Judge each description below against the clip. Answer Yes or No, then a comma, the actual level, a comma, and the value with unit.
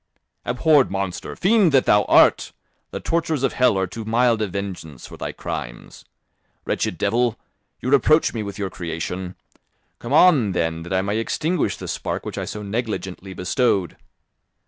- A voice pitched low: Yes, low, 105 Hz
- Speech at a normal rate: Yes, average, 165 wpm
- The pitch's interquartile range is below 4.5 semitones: No, wide, 5.4 semitones